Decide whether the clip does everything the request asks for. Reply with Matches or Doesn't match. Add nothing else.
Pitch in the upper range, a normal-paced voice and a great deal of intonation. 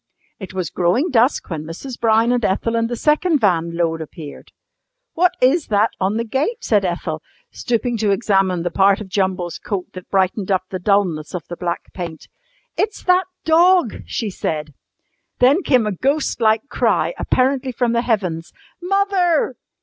Matches